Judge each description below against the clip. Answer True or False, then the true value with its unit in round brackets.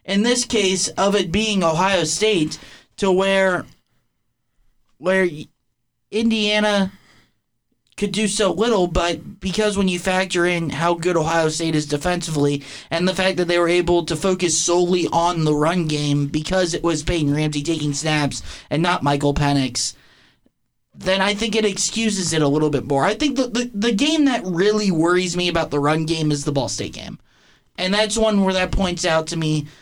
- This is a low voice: False (175 Hz)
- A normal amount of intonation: True (4.1 semitones)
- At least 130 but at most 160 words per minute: False (185 wpm)